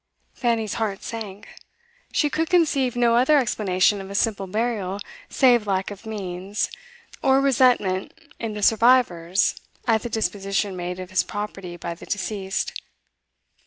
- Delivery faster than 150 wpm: No, average, 140 wpm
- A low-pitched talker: No, high, 210 Hz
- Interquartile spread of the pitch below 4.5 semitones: Yes, average, 3.9 semitones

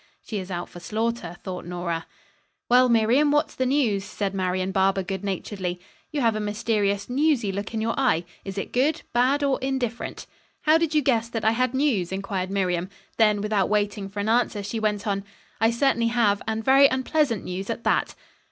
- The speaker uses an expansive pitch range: No, average, 4.3 semitones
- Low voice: No, high, 215 Hz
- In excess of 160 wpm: Yes, average, 195 wpm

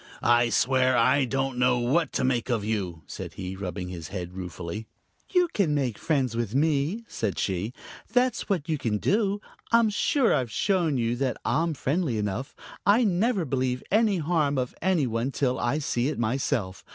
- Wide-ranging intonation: Yes, wide, 6.5 semitones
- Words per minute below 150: No, average, 180 wpm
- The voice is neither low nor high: No, low, 130 Hz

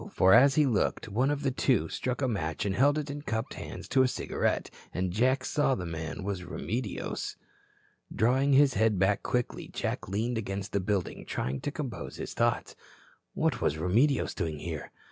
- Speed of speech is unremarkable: Yes, average, 185 wpm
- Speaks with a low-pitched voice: Yes, low, 110 Hz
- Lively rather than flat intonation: Yes, wide, 6.1 semitones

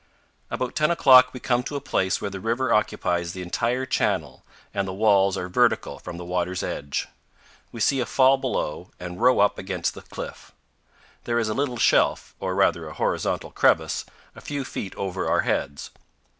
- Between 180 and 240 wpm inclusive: Yes, average, 185 wpm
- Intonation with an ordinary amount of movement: No, wide, 5.8 semitones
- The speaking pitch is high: No, low, 105 Hz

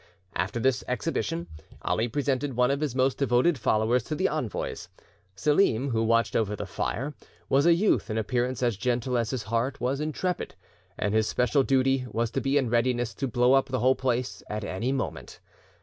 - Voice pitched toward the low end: Yes, low, 125 Hz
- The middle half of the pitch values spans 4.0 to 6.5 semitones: No, average, 2.8 semitones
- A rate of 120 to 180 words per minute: No, average, 190 wpm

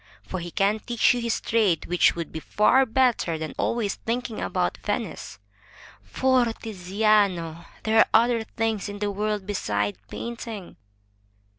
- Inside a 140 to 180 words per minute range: Yes, average, 150 wpm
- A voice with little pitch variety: No, average, 4.4 semitones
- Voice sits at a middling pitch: No, high, 210 Hz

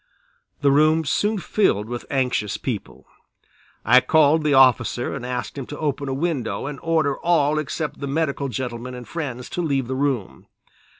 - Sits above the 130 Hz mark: Yes, medium, 140 Hz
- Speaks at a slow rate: No, average, 170 wpm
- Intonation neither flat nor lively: Yes, average, 3.5 semitones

